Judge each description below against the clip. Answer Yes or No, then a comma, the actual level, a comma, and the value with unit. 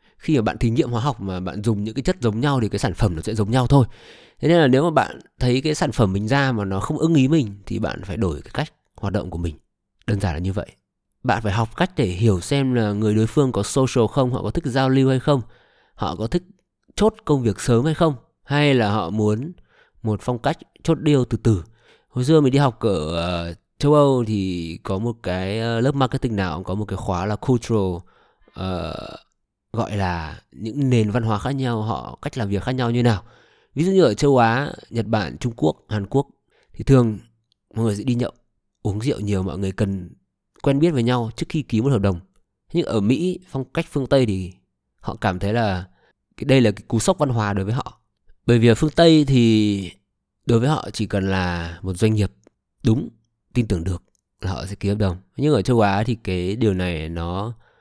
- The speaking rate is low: No, average, 240 wpm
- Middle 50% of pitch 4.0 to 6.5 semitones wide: Yes, average, 5.1 semitones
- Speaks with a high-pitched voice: No, low, 115 Hz